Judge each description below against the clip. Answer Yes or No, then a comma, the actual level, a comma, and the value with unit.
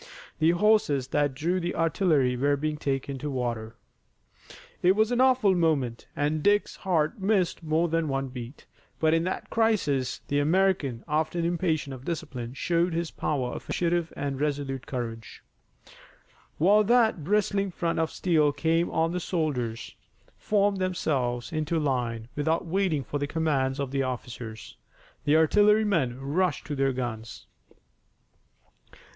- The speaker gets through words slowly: No, average, 145 wpm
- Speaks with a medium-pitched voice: Yes, medium, 155 Hz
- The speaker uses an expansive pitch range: No, average, 4.7 semitones